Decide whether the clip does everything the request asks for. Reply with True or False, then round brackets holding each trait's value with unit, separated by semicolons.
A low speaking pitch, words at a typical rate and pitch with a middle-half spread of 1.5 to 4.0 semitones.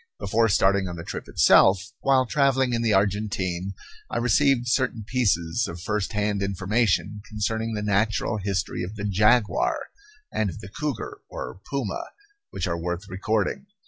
True (105 Hz; 155 wpm; 3.3 semitones)